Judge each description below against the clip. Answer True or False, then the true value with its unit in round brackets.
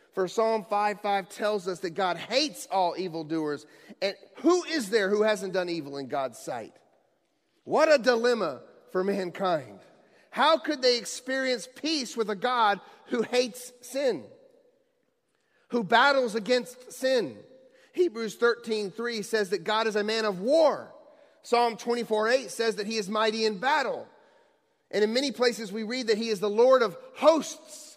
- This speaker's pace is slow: False (160 wpm)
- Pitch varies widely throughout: False (4.3 semitones)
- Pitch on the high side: True (230 Hz)